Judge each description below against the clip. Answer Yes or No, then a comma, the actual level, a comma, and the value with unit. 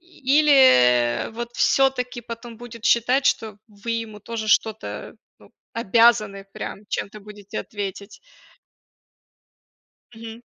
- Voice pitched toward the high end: Yes, high, 225 Hz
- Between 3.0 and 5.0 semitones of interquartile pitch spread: No, narrow, 2.6 semitones